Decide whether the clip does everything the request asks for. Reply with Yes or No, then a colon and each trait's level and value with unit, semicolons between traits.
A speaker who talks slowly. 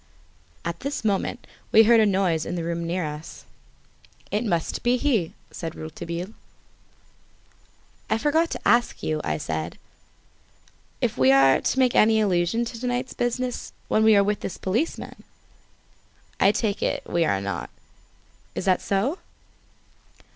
No: average, 150 wpm